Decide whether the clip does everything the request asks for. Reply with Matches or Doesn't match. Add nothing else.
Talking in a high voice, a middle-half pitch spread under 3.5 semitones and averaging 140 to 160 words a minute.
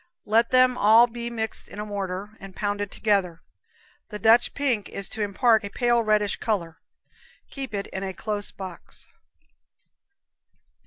Matches